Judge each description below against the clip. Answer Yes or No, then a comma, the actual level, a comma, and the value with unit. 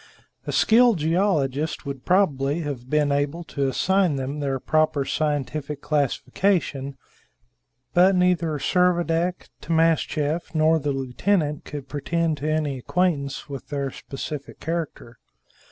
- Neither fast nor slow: No, slow, 120 wpm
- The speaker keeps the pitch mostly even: No, average, 3.3 semitones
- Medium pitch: Yes, medium, 150 Hz